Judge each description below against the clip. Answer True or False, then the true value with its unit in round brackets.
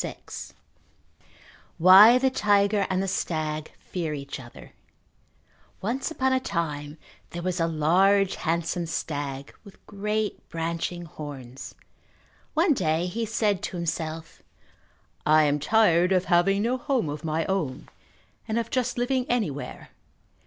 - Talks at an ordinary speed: False (130 wpm)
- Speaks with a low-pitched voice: False (180 Hz)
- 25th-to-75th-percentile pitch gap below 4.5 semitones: False (5.2 semitones)